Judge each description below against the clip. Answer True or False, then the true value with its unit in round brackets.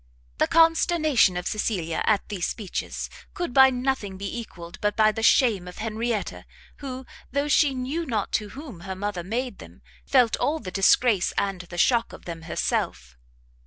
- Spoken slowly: False (170 wpm)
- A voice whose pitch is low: False (220 Hz)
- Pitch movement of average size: False (5.7 semitones)